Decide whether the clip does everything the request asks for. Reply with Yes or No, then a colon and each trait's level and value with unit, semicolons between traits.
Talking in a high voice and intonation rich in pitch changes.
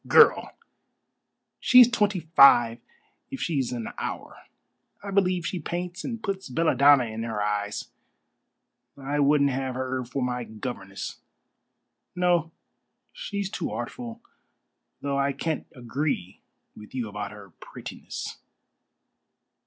No: medium, 140 Hz; wide, 7.2 semitones